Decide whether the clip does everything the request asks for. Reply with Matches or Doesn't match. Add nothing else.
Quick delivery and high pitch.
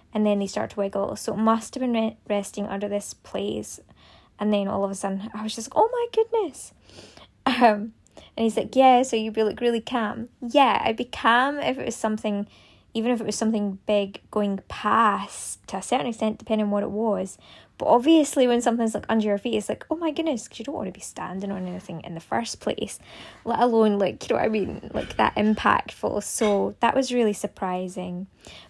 Matches